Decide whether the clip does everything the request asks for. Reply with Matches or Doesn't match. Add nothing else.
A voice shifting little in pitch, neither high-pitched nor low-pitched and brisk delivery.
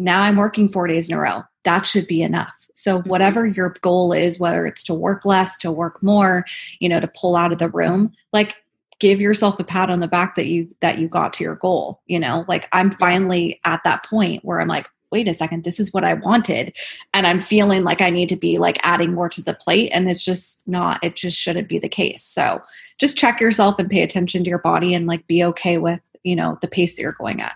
Matches